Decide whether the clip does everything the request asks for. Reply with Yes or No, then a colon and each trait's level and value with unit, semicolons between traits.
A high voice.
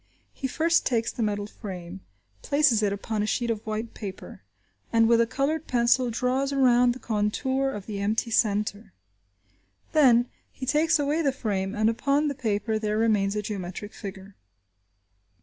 Yes: high, 230 Hz